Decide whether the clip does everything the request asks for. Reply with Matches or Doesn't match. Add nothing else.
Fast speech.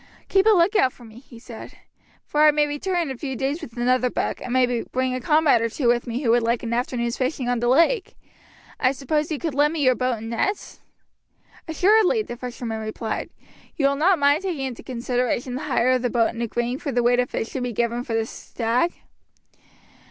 Matches